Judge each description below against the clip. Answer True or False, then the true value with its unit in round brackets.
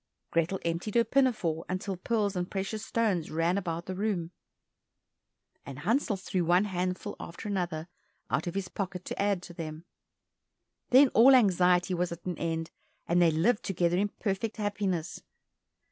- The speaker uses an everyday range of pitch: True (3.2 semitones)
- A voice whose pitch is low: False (185 Hz)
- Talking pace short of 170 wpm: True (160 wpm)